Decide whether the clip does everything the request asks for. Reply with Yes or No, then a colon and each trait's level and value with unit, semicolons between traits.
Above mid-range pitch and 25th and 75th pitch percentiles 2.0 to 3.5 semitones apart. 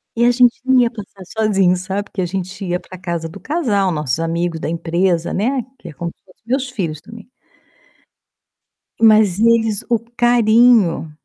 No: high, 200 Hz; average, 5.0 semitones